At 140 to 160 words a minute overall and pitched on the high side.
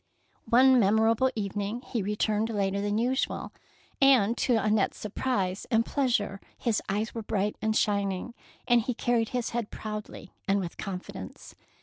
Yes: average, 150 wpm; high, 215 Hz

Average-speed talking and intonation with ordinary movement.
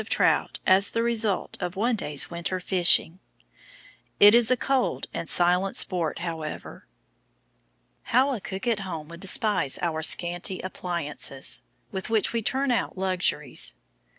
Yes: average, 145 wpm; average, 4.4 semitones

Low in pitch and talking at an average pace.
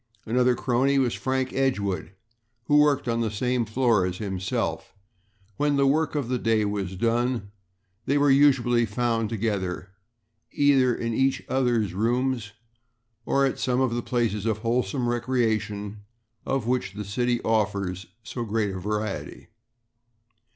Yes: low, 115 Hz; average, 145 wpm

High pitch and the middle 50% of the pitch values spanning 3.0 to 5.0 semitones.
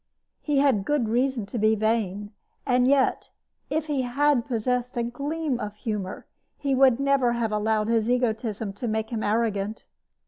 Yes: high, 235 Hz; average, 3.5 semitones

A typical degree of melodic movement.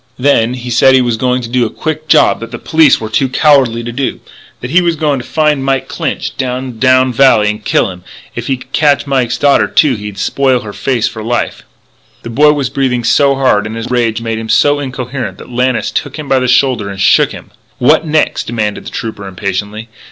Yes: average, 3.3 semitones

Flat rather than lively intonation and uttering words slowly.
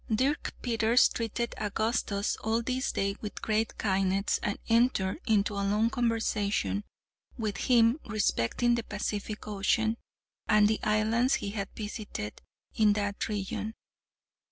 Yes: narrow, 2.1 semitones; slow, 130 wpm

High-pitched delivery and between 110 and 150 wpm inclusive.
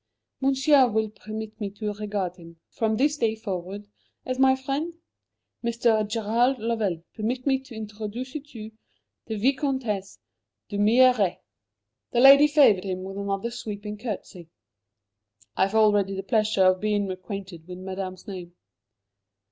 Yes: high, 215 Hz; average, 140 wpm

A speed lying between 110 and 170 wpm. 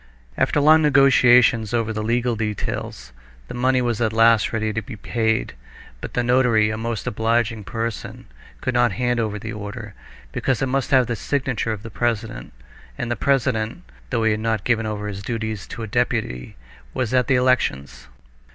No: average, 180 wpm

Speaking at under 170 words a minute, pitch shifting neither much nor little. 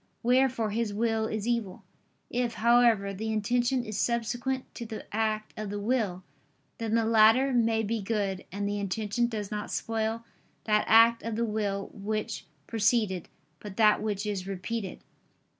No: average, 160 wpm; narrow, 2.1 semitones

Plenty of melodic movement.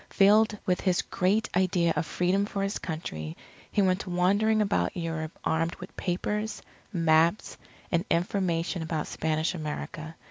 No: average, 3.3 semitones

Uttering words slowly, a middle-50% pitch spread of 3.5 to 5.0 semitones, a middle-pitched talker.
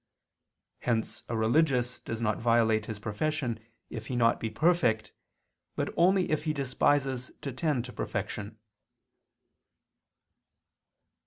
No: slow, 115 wpm; average, 4.6 semitones; low, 120 Hz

